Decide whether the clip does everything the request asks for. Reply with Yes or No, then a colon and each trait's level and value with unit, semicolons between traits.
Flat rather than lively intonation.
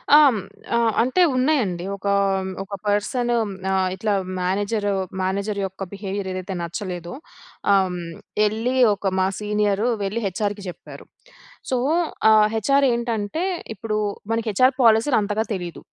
No: average, 3.1 semitones